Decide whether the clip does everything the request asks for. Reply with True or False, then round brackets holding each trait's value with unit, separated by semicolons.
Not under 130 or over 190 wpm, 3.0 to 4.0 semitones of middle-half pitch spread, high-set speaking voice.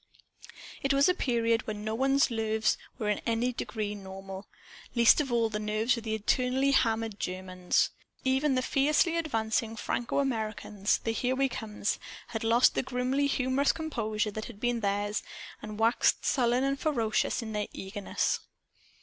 True (160 wpm; 3.6 semitones; 230 Hz)